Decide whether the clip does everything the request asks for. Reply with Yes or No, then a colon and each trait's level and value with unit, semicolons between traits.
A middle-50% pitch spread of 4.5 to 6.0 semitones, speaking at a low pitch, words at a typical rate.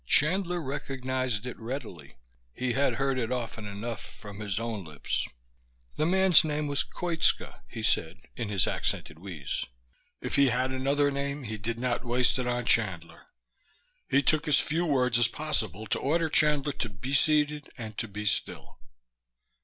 Yes: average, 4.8 semitones; low, 125 Hz; average, 165 wpm